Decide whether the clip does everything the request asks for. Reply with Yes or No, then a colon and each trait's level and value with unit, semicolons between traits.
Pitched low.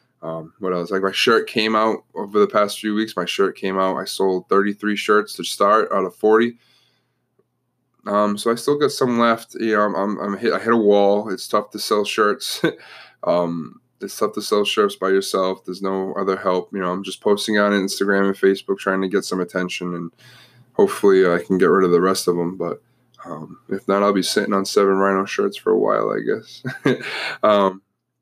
Yes: low, 100 Hz